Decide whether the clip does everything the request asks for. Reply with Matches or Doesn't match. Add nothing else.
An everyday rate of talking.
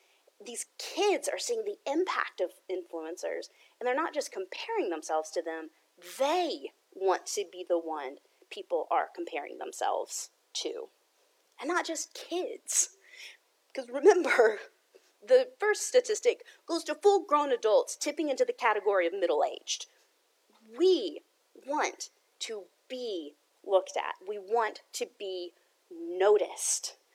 Doesn't match